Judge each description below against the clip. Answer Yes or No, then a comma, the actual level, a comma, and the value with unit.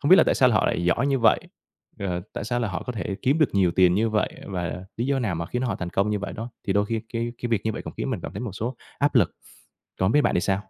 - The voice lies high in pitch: No, low, 110 Hz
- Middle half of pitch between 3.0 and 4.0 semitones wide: No, average, 4.4 semitones